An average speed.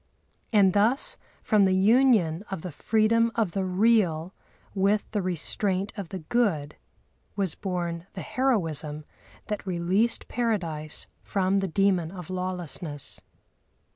No: slow, 125 wpm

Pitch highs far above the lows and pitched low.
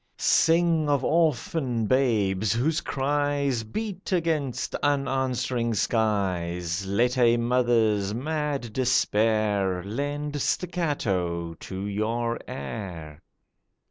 Yes: wide, 6.0 semitones; low, 120 Hz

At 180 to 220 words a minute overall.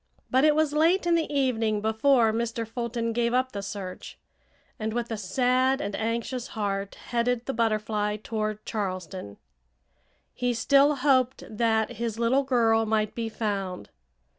No: average, 150 wpm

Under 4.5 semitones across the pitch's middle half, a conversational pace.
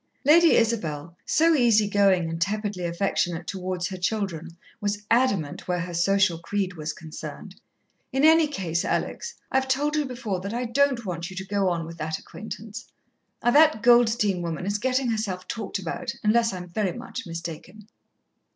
No: average, 5.2 semitones; average, 165 wpm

